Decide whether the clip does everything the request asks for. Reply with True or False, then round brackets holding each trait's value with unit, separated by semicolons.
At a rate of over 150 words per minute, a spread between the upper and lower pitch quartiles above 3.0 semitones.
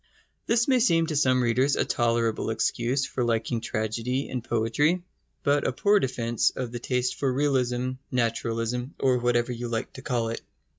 False (170 wpm; 2.6 semitones)